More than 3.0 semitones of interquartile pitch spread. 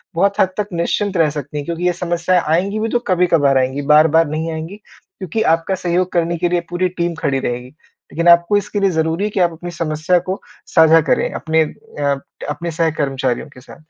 No: average, 2.7 semitones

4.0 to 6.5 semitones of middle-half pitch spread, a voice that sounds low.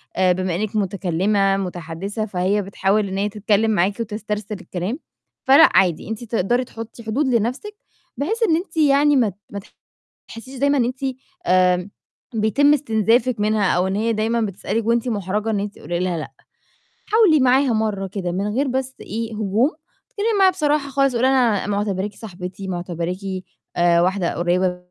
No: average, 5.0 semitones; high, 215 Hz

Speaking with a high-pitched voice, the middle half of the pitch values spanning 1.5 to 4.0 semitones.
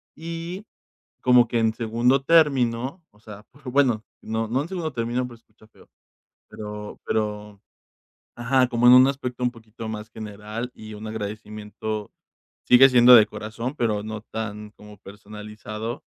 No: low, 115 Hz; average, 2.8 semitones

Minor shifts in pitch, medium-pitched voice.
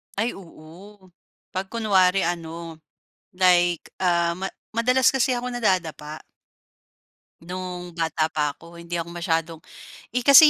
No: average, 3.4 semitones; medium, 180 Hz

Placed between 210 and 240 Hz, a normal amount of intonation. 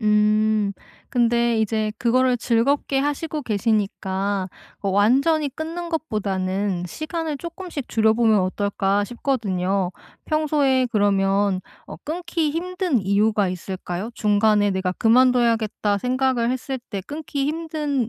No: high, 230 Hz; wide, 5.7 semitones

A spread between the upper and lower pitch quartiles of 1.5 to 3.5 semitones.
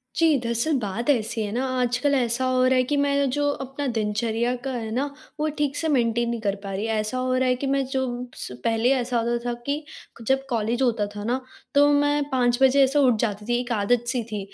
Yes: average, 2.8 semitones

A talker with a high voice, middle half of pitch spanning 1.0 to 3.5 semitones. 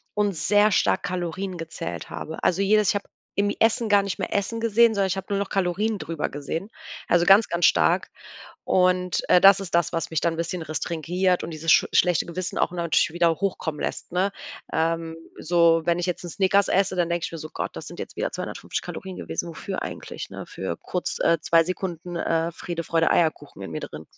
No: medium, 175 Hz; average, 2.8 semitones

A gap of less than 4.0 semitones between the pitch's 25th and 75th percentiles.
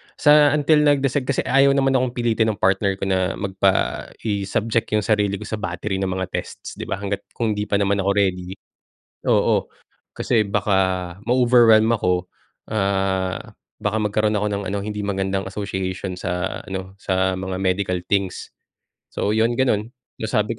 Yes: average, 2.7 semitones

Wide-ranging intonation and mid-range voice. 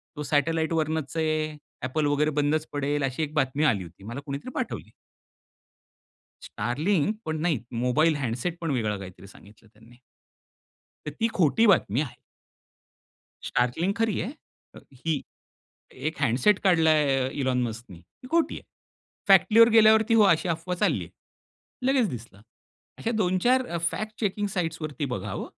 Yes: wide, 6.0 semitones; medium, 155 Hz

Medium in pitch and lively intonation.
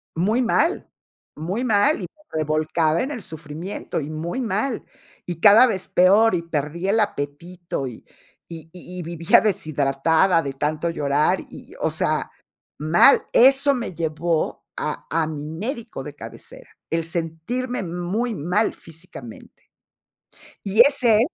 Yes: medium, 175 Hz; wide, 5.8 semitones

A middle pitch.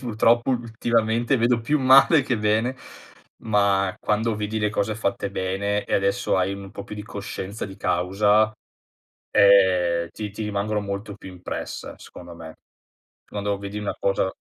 No: low, 105 Hz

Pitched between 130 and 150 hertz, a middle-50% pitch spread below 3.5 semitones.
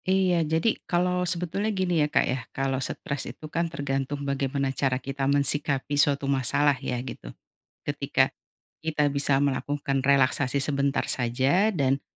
Yes: medium, 140 Hz; average, 3.0 semitones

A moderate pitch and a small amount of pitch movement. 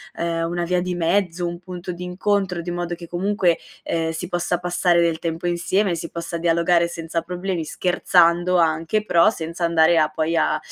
Yes: medium, 175 Hz; narrow, 1.2 semitones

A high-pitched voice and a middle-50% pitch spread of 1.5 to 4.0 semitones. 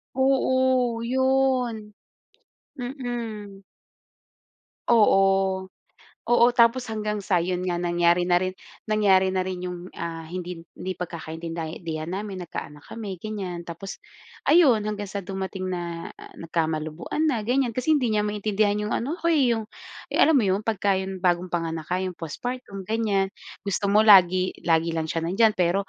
No: high, 195 Hz; average, 4.4 semitones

